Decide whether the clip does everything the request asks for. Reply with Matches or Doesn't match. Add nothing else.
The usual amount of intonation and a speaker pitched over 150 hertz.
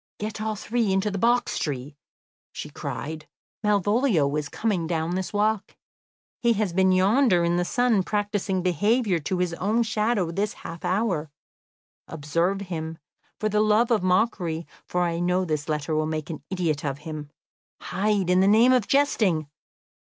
Matches